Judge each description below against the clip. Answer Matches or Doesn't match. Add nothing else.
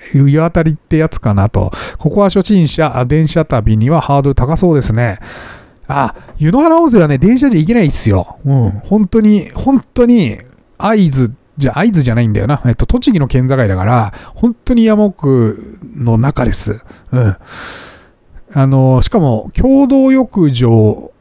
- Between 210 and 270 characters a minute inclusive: Doesn't match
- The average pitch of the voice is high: Doesn't match